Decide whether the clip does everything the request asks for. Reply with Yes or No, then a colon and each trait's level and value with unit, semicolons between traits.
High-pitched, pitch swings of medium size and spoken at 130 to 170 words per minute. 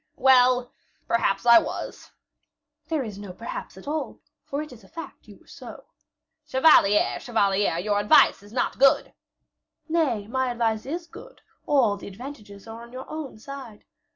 Yes: high, 240 Hz; average, 4.9 semitones; average, 160 wpm